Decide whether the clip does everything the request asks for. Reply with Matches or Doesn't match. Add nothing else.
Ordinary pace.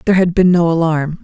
Doesn't match